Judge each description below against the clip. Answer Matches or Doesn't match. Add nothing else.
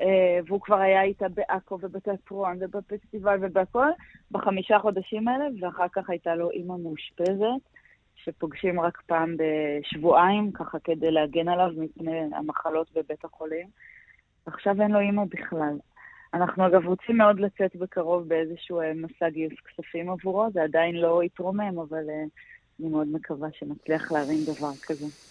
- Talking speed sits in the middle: Matches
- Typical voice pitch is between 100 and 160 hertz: Doesn't match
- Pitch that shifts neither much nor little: Matches